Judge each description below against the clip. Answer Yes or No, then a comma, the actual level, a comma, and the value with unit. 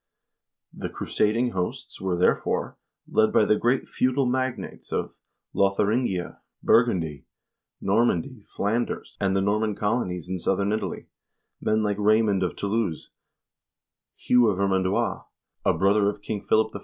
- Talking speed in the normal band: No, slow, 130 wpm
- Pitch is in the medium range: No, low, 105 Hz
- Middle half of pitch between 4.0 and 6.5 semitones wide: No, average, 2.8 semitones